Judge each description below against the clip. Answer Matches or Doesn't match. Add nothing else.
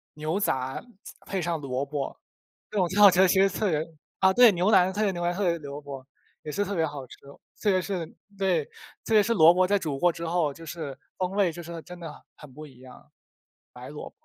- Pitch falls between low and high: Matches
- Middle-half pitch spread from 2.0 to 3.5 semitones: Doesn't match